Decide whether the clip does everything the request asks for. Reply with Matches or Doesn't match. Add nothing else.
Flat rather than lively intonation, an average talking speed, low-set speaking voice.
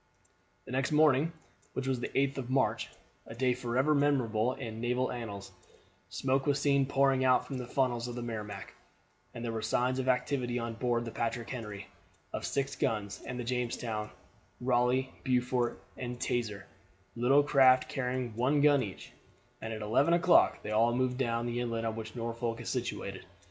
Matches